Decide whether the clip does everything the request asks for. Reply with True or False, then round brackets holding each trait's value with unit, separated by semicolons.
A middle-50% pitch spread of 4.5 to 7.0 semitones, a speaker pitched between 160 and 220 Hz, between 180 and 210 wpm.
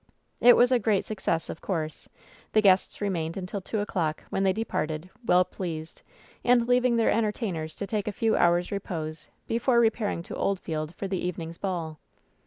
True (4.8 semitones; 190 Hz; 185 wpm)